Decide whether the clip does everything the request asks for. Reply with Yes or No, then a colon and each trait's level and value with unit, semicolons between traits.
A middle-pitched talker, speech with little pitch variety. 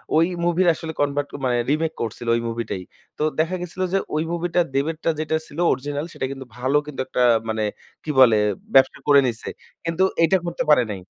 No: medium, 145 Hz; average, 4.3 semitones